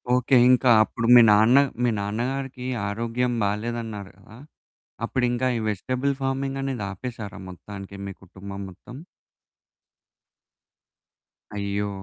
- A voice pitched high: No, low, 115 Hz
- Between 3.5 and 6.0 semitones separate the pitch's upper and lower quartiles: Yes, average, 4.0 semitones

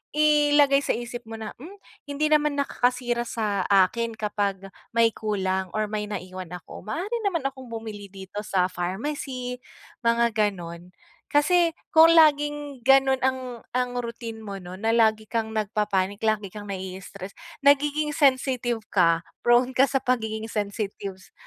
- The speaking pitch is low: No, high, 230 Hz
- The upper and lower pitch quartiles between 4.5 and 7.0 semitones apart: Yes, average, 4.9 semitones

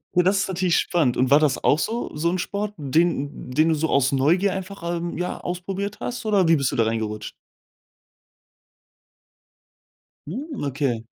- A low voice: No, medium, 170 Hz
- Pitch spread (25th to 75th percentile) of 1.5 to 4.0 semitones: No, wide, 5.4 semitones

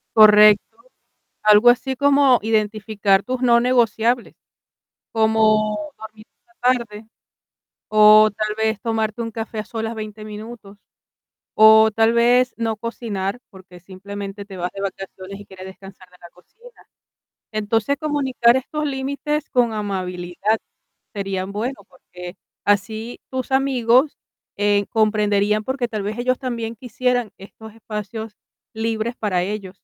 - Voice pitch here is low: No, high, 220 Hz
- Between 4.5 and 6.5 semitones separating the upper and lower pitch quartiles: No, average, 2.8 semitones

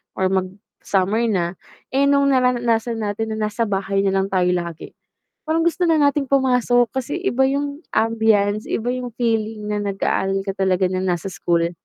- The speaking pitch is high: Yes, high, 220 Hz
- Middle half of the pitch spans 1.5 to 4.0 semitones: No, average, 4.7 semitones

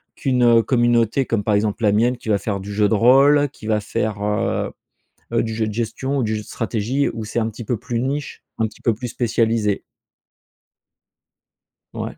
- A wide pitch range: No, narrow, 2.5 semitones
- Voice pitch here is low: Yes, low, 115 Hz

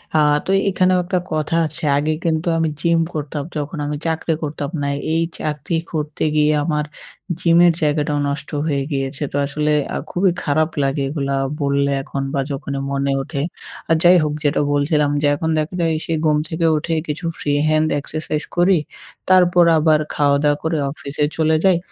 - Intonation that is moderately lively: No, narrow, 2.2 semitones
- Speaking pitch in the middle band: Yes, medium, 150 Hz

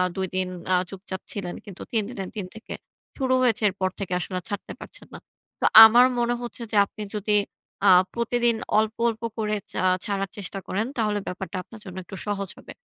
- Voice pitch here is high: Yes, high, 205 Hz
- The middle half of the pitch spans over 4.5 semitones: No, average, 2.9 semitones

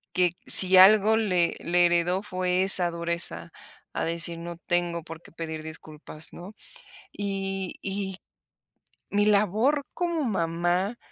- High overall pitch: No, medium, 180 Hz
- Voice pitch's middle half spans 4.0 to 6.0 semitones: No, average, 2.8 semitones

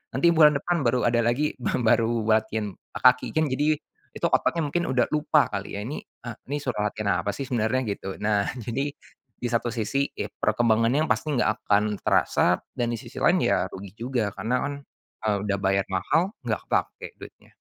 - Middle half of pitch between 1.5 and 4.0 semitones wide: No, average, 4.7 semitones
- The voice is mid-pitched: No, low, 120 Hz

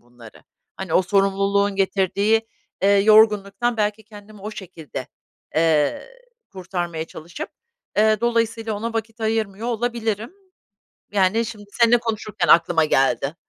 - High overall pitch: Yes, high, 205 Hz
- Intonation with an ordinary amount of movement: Yes, average, 3.3 semitones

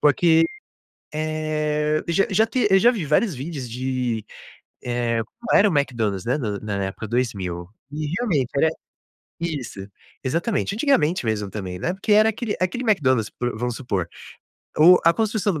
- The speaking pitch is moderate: Yes, medium, 150 Hz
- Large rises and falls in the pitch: Yes, wide, 7.5 semitones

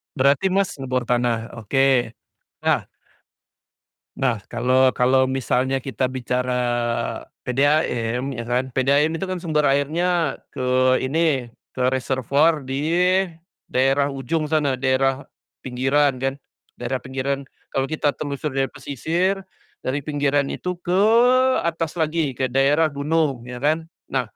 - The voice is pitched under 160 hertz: Yes, low, 135 Hz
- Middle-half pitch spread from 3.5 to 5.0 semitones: No, average, 2.8 semitones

